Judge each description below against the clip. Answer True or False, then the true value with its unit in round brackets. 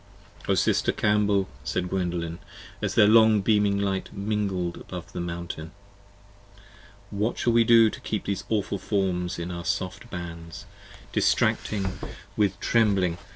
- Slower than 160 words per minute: True (150 wpm)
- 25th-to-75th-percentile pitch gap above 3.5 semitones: False (2.9 semitones)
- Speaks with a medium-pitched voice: False (100 Hz)